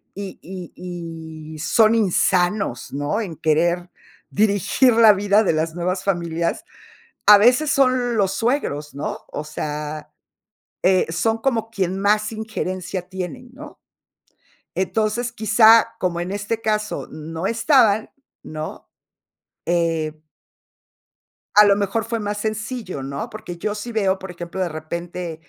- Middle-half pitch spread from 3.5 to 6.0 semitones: Yes, average, 4.4 semitones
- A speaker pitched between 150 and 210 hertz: Yes, high, 190 Hz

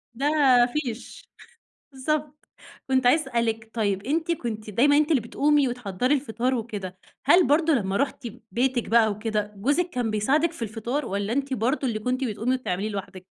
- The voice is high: Yes, high, 245 Hz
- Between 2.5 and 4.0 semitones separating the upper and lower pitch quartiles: No, average, 4.8 semitones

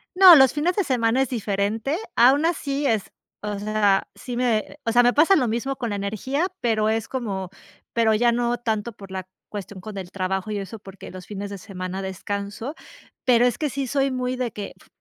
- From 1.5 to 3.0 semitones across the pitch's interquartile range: No, average, 4.2 semitones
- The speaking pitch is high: Yes, high, 225 Hz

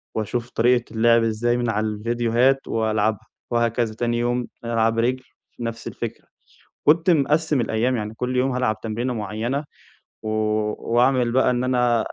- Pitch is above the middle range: No, low, 120 Hz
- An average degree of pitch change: No, narrow, 2.0 semitones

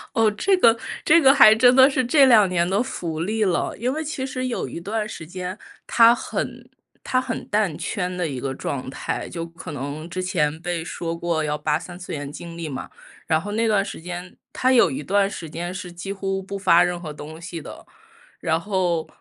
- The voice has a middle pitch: Yes, medium, 180 Hz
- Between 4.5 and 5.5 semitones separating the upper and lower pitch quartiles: Yes, average, 5.0 semitones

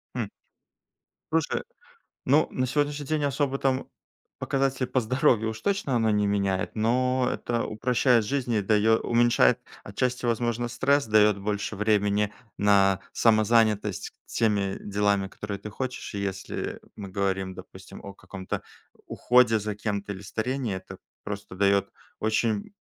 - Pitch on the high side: No, low, 110 Hz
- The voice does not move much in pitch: No, average, 3.9 semitones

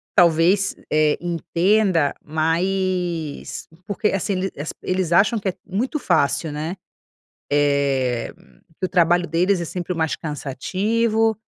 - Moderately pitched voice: Yes, medium, 175 Hz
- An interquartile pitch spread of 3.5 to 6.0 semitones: Yes, average, 3.8 semitones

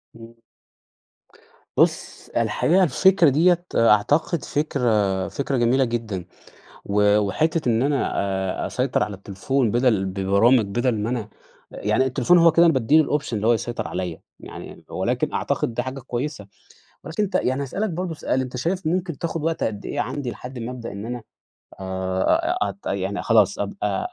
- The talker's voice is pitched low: Yes, low, 125 Hz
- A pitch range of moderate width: No, wide, 6.5 semitones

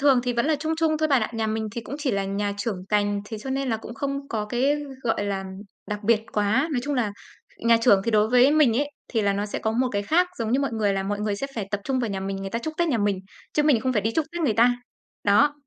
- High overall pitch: Yes, high, 230 Hz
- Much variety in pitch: No, average, 5.0 semitones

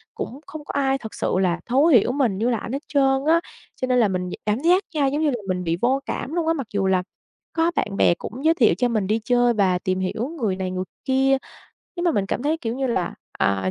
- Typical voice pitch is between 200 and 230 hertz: No, high, 245 Hz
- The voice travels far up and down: Yes, wide, 6.4 semitones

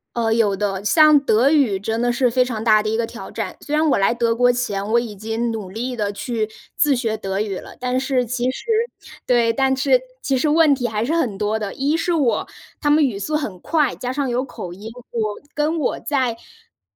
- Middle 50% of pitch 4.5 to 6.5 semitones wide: No, average, 4.1 semitones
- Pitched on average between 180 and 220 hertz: No, high, 240 Hz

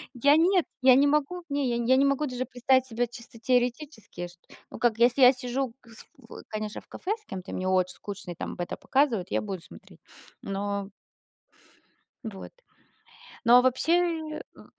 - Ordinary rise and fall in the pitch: Yes, average, 4.5 semitones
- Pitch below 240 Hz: No, high, 245 Hz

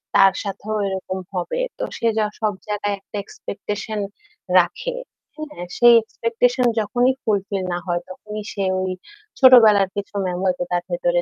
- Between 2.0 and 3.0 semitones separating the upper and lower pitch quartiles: No, average, 3.4 semitones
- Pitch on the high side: Yes, high, 205 Hz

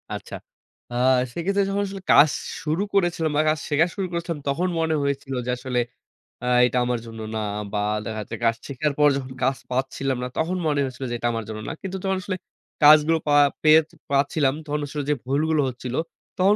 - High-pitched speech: No, medium, 150 Hz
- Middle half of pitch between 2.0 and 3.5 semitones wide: No, average, 4.1 semitones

